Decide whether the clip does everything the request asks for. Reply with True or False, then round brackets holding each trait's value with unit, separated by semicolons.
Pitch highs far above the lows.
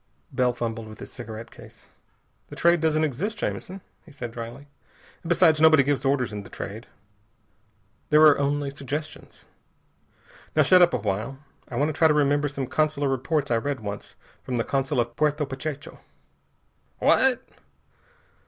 False (4.4 semitones)